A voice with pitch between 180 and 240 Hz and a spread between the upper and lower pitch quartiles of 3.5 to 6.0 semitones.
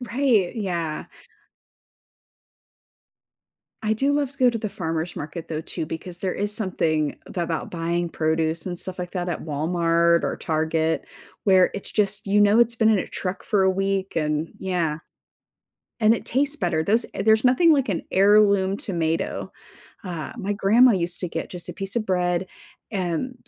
Yes: medium, 185 Hz; average, 4.2 semitones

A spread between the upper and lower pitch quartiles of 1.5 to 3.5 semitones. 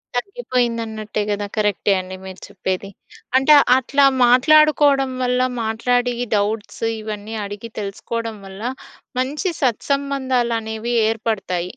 No: average, 3.9 semitones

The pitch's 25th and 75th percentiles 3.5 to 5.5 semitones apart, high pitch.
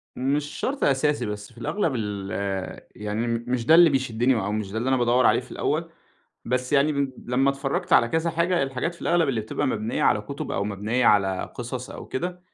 No: average, 4.2 semitones; low, 125 Hz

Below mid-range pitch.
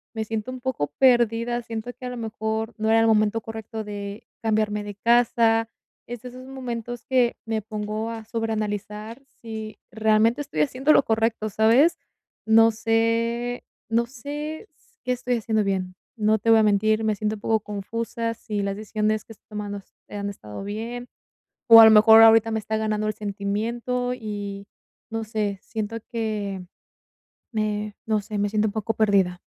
No: high, 220 Hz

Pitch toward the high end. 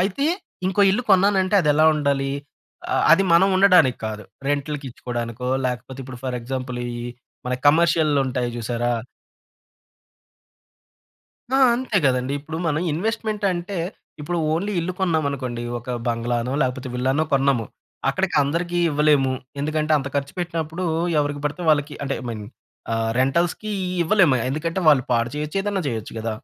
No: medium, 145 Hz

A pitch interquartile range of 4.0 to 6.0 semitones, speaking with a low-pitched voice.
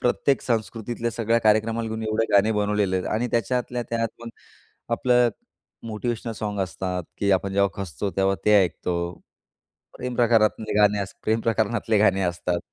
No: narrow, 2.6 semitones; low, 110 Hz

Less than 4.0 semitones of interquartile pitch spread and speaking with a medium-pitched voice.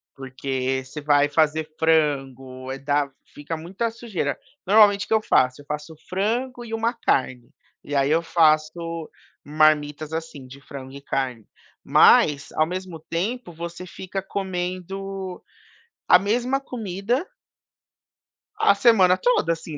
No: average, 5.3 semitones; medium, 165 Hz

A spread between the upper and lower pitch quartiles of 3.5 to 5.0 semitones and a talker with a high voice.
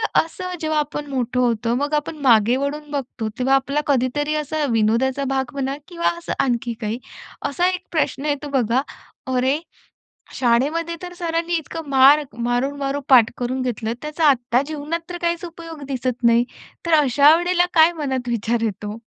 Yes: average, 4.2 semitones; very high, 275 Hz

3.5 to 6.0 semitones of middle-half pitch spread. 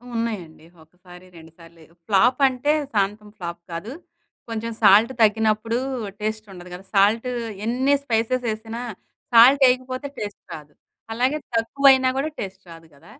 Yes: average, 5.2 semitones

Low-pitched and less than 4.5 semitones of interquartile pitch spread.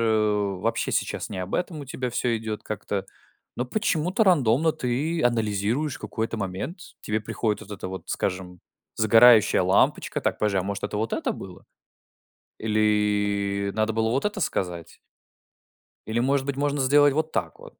No: low, 110 Hz; average, 5.2 semitones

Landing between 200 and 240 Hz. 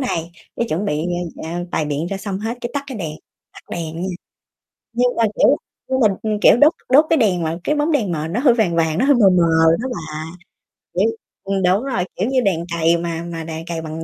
No: high, 190 Hz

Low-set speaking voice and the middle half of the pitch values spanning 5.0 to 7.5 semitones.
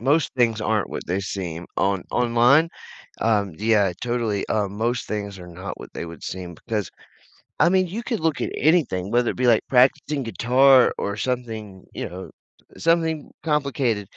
Yes: low, 115 Hz; wide, 5.4 semitones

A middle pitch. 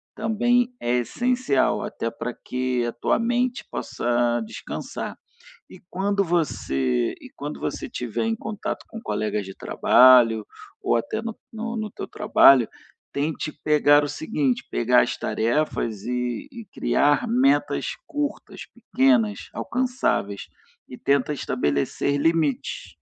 Yes: medium, 145 Hz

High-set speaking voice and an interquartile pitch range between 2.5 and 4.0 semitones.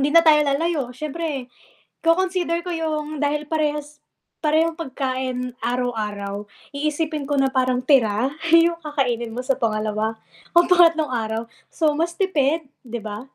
No: very high, 285 Hz; average, 4.6 semitones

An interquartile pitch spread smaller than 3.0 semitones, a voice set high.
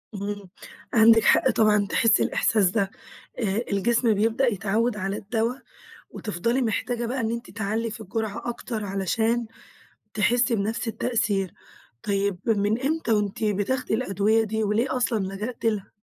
Yes: narrow, 2.5 semitones; high, 220 Hz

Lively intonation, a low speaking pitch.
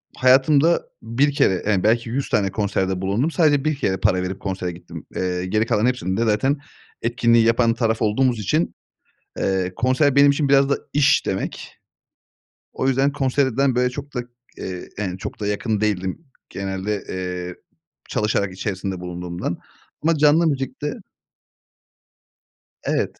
Yes: wide, 6.2 semitones; low, 115 Hz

